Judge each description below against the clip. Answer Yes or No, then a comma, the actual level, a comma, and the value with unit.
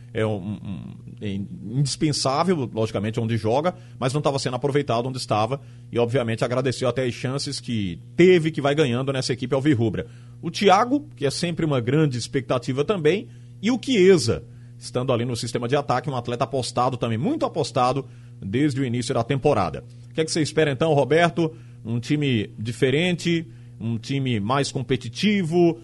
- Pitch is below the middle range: Yes, low, 130 Hz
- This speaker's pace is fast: No, average, 170 wpm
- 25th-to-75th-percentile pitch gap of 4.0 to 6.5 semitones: No, average, 3.5 semitones